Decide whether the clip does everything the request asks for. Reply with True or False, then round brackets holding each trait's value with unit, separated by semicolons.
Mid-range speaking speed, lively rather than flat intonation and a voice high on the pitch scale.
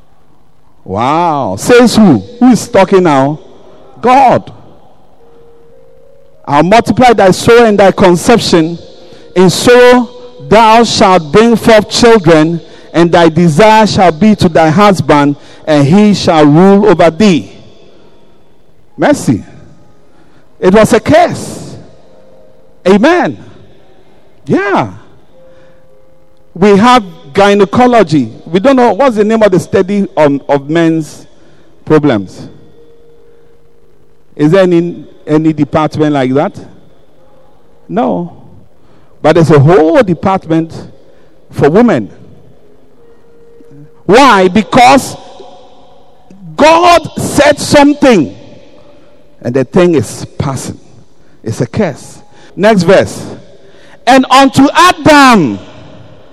False (100 wpm; 7.7 semitones; 195 Hz)